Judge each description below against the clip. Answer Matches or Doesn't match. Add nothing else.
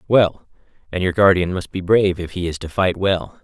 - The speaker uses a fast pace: Matches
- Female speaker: Doesn't match